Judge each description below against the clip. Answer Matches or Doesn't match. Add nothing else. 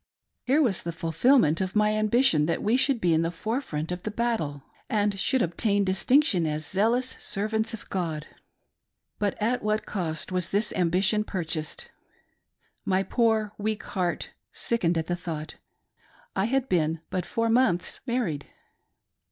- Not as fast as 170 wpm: Matches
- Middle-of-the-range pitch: Doesn't match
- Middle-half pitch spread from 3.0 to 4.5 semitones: Doesn't match